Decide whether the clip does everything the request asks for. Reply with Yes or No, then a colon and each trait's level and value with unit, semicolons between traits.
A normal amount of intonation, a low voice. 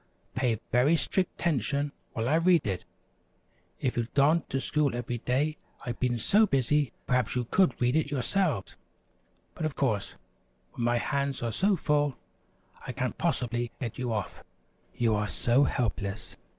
Yes: average, 3.9 semitones; low, 130 Hz